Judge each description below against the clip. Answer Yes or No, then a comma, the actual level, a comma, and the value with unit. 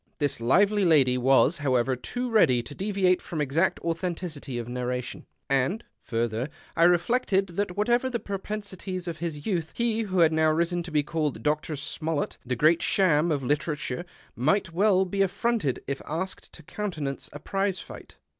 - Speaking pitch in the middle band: Yes, medium, 165 Hz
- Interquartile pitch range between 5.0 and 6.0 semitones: Yes, average, 5.3 semitones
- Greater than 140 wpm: Yes, average, 170 wpm